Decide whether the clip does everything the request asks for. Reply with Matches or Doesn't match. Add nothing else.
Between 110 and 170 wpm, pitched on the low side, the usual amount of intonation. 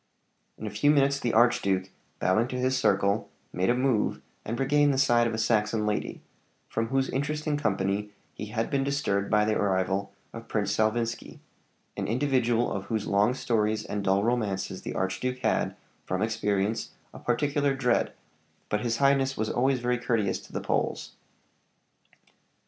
Matches